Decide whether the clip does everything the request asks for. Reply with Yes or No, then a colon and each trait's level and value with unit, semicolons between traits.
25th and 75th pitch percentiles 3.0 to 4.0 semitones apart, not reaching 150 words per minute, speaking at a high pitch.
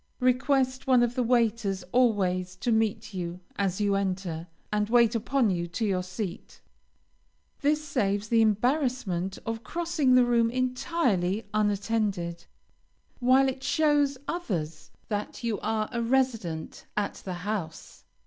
No: average, 4.8 semitones; slow, 135 wpm; high, 220 Hz